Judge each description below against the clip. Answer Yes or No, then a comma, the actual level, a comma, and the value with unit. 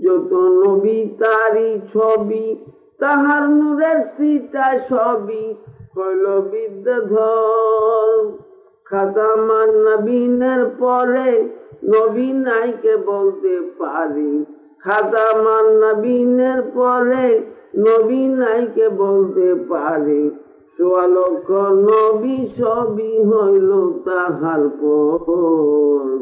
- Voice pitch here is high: Yes, high, 220 Hz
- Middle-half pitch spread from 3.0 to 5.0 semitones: Yes, average, 4.6 semitones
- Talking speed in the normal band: Yes, average, 80 wpm